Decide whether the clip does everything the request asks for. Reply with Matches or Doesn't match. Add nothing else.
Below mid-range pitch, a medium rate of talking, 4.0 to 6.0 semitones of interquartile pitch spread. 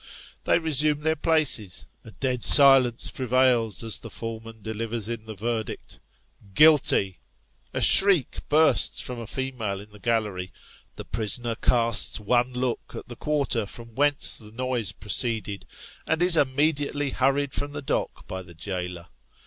Matches